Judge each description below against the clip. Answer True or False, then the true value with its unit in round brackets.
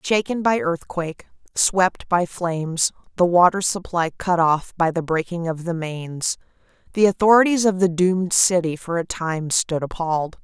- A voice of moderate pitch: True (175 Hz)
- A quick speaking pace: False (160 wpm)